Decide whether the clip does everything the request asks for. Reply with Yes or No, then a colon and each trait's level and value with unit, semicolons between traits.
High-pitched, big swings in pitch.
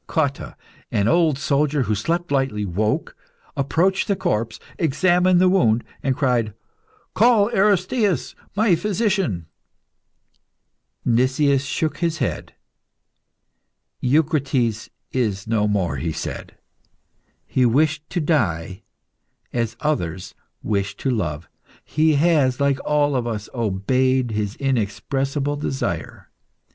No: low, 135 Hz; wide, 6.6 semitones